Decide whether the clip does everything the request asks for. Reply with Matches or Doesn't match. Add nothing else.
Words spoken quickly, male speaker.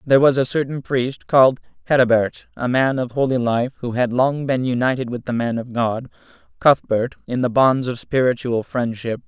Doesn't match